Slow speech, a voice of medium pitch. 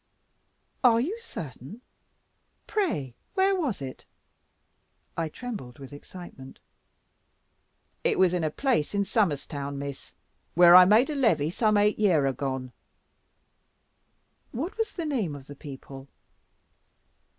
Yes: slow, 125 wpm; medium, 180 Hz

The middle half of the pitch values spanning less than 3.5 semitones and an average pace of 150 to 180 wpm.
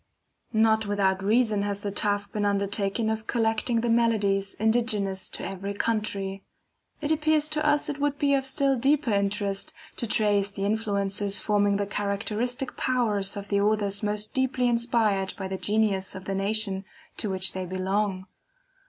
Yes: average, 2.7 semitones; average, 160 wpm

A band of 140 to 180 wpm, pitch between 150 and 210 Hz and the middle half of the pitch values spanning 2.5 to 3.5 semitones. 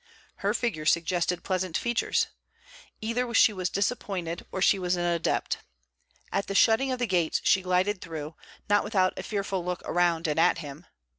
Yes: average, 170 wpm; medium, 185 Hz; average, 3.2 semitones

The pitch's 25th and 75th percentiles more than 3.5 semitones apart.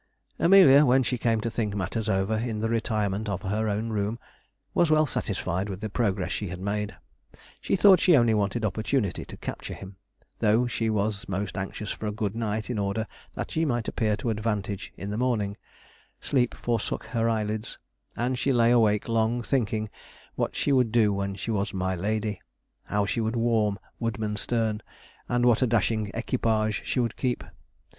No: narrow, 2.5 semitones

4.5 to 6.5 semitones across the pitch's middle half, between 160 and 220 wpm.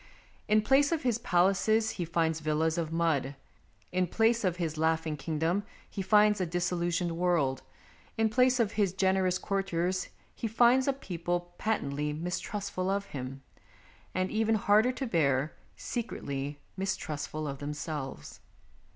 No: average, 5.1 semitones; average, 140 wpm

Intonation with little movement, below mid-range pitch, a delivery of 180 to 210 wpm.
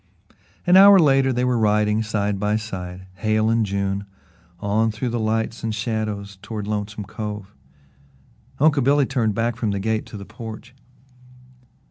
No: narrow, 2.3 semitones; low, 110 Hz; average, 155 wpm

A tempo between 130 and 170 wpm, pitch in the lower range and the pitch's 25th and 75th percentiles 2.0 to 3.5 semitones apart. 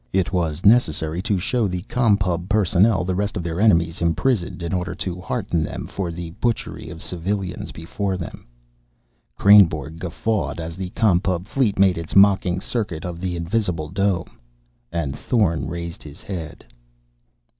Yes: average, 160 wpm; very low, 90 Hz; average, 3.2 semitones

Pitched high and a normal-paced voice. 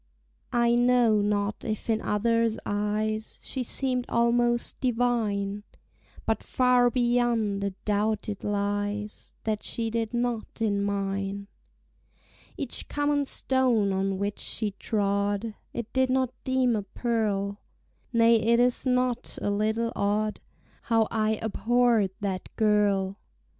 No: high, 220 Hz; slow, 125 wpm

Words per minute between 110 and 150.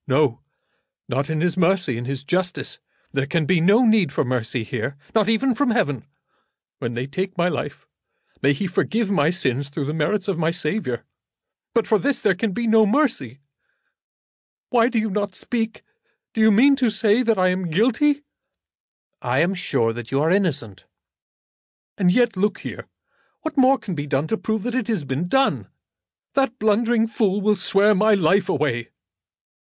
No: average, 180 wpm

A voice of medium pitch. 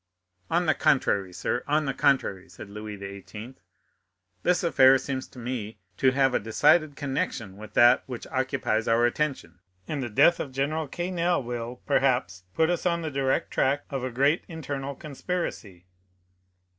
No: low, 130 Hz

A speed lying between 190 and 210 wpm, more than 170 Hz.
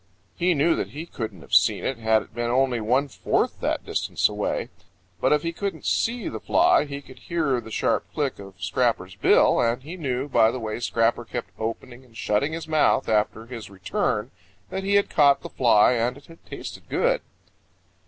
No: average, 200 wpm; low, 125 Hz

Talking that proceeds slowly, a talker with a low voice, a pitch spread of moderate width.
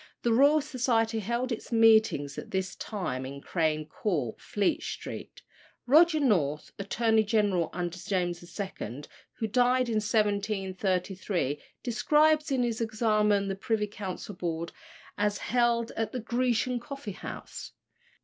No: slow, 130 wpm; high, 215 Hz; average, 4.3 semitones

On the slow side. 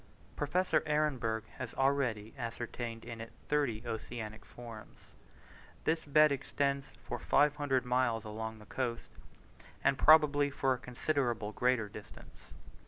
Yes: slow, 120 wpm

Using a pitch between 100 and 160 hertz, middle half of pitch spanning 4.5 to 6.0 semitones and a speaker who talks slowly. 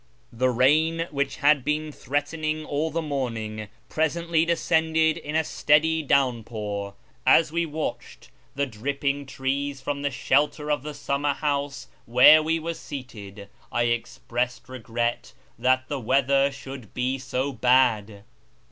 No: medium, 140 Hz; average, 3.4 semitones; slow, 130 wpm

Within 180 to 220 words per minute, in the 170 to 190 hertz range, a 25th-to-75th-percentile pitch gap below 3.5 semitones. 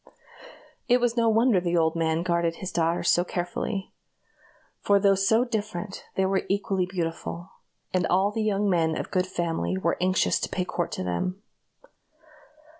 No: average, 165 wpm; medium, 185 Hz; average, 2.9 semitones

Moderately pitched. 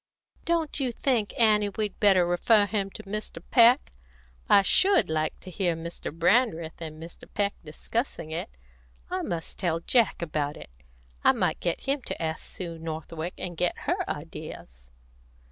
Yes: medium, 180 Hz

